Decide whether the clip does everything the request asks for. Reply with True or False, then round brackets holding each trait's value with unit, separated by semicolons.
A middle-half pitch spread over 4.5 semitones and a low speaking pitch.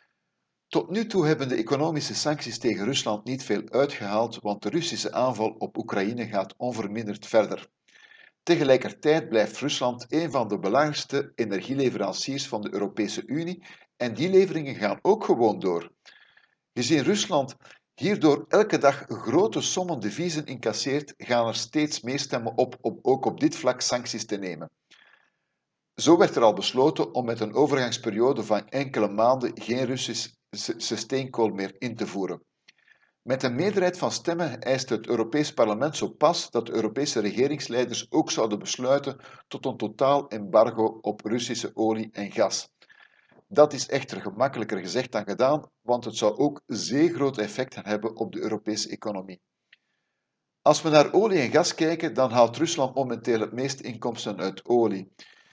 True (4.9 semitones; 130 Hz)